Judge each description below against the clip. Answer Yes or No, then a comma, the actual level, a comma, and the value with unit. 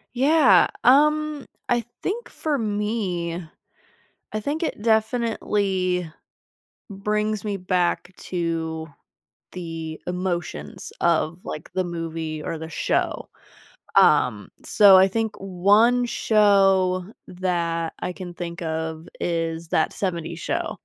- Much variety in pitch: No, average, 4.2 semitones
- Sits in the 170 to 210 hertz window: Yes, medium, 185 Hz